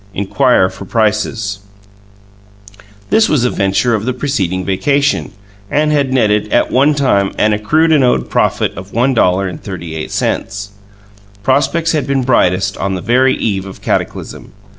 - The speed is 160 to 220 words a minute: No, average, 140 wpm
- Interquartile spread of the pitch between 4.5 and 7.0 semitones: Yes, wide, 5.6 semitones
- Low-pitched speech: Yes, low, 110 Hz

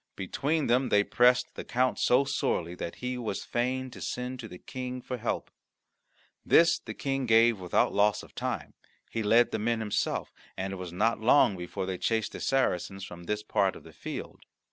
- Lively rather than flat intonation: No, average, 4.6 semitones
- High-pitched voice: No, low, 115 Hz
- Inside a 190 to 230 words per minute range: Yes, average, 195 wpm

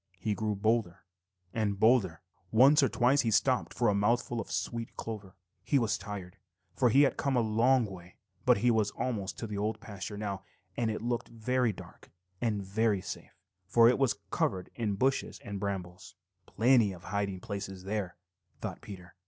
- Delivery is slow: No, average, 175 wpm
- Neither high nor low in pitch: No, low, 110 Hz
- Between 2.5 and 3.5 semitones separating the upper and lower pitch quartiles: Yes, average, 3.2 semitones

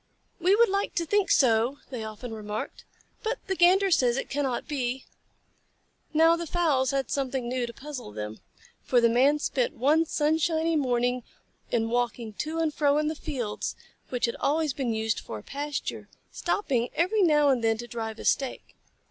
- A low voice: No, very high, 270 Hz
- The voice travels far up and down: No, average, 5.0 semitones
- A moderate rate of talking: Yes, average, 180 wpm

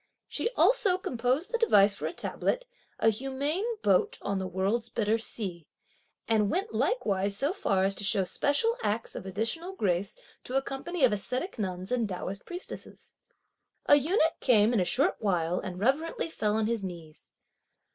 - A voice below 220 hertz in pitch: No, high, 225 Hz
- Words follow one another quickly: No, average, 170 wpm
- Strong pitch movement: Yes, wide, 7.8 semitones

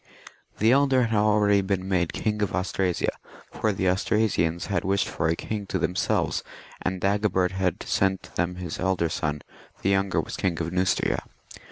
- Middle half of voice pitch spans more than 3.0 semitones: No, narrow, 2.4 semitones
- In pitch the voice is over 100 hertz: No, very low, 95 Hz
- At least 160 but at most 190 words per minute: Yes, average, 175 wpm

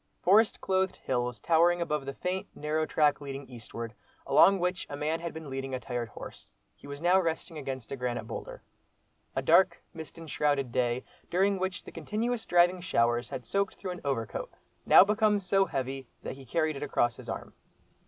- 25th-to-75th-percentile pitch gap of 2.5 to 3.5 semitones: No, wide, 5.6 semitones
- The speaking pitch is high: No, medium, 155 Hz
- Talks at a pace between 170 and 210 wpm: Yes, average, 185 wpm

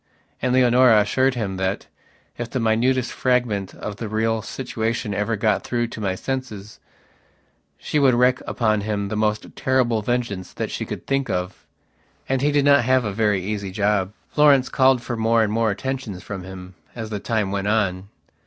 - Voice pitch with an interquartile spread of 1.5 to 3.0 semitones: No, average, 3.7 semitones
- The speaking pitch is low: Yes, low, 110 Hz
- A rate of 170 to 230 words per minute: Yes, average, 180 wpm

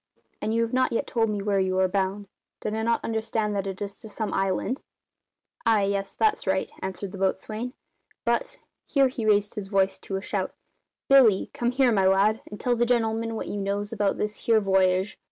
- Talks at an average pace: No, fast, 210 wpm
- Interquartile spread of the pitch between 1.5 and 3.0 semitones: Yes, average, 2.7 semitones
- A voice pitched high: Yes, high, 210 Hz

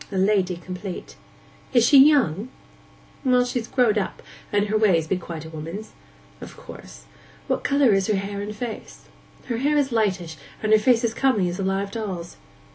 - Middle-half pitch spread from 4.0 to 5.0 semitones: Yes, average, 4.4 semitones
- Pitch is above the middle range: Yes, high, 210 Hz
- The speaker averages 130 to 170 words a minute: No, average, 185 wpm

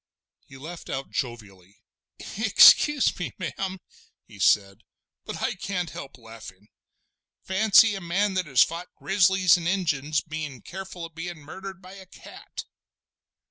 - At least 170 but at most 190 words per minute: No, average, 140 wpm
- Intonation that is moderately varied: No, wide, 6.0 semitones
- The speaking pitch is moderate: Yes, medium, 170 Hz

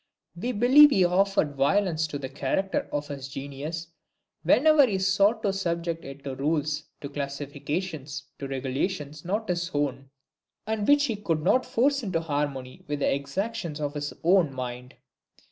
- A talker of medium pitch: Yes, medium, 160 Hz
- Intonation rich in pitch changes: Yes, wide, 5.7 semitones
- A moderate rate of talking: Yes, average, 160 wpm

